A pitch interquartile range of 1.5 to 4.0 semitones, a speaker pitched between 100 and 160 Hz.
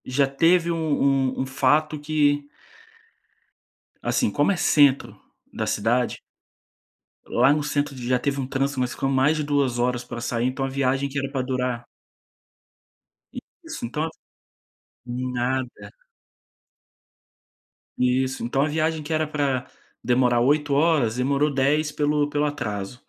Yes: average, 2.7 semitones; low, 135 Hz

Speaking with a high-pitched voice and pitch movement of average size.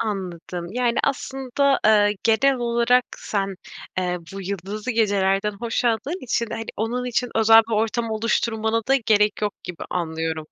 Yes: high, 220 Hz; average, 3.2 semitones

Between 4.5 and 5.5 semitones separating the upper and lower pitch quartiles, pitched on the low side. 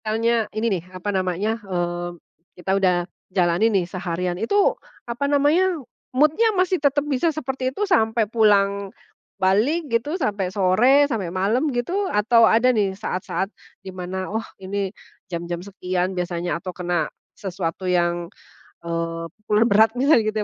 No: average, 5.2 semitones; high, 205 Hz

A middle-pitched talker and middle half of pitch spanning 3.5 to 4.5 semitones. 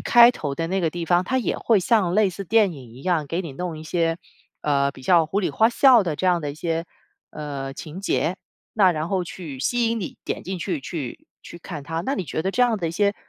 Yes: medium, 175 Hz; average, 4.2 semitones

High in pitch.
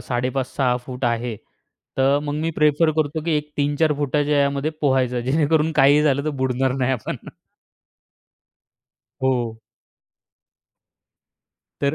No: medium, 140 Hz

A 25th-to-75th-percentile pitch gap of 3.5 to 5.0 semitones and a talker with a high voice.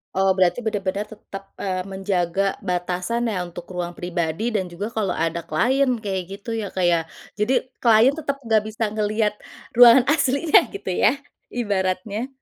Yes: average, 4.1 semitones; high, 200 Hz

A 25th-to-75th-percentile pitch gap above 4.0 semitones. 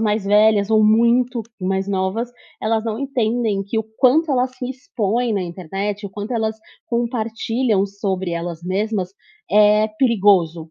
No: average, 3.2 semitones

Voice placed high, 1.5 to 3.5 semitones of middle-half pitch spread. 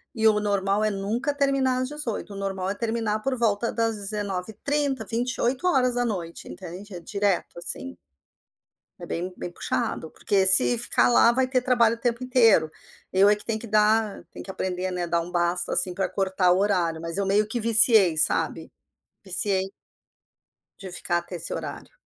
No: high, 205 Hz; average, 4.0 semitones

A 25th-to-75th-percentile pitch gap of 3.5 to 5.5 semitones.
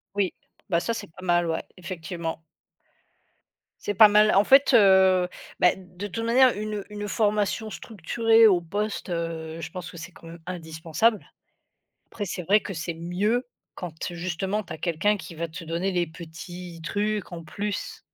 Yes: average, 3.8 semitones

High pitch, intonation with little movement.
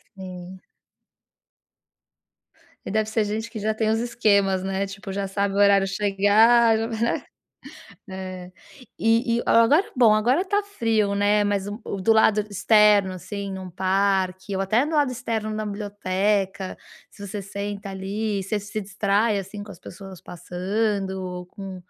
Yes: high, 205 Hz; narrow, 2.1 semitones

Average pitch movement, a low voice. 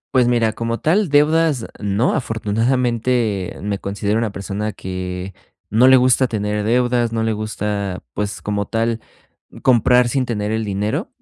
Yes: average, 3.1 semitones; low, 110 Hz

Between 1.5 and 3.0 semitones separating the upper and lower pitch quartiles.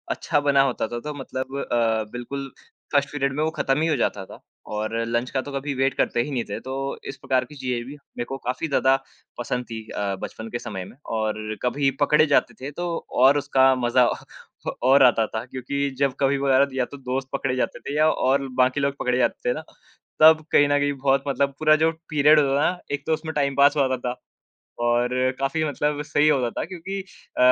Yes: narrow, 2.4 semitones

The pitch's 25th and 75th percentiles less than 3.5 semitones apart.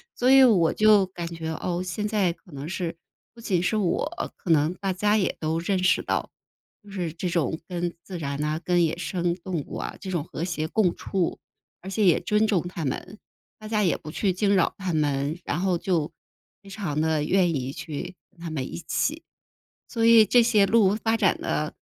No: average, 3.9 semitones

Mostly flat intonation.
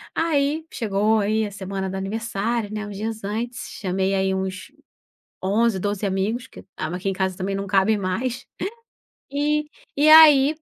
No: average, 3.9 semitones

